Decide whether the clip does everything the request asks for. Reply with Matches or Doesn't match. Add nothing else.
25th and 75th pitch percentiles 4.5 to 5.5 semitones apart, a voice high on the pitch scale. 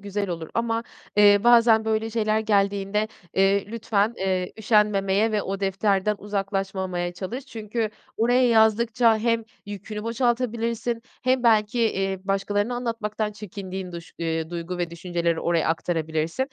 Doesn't match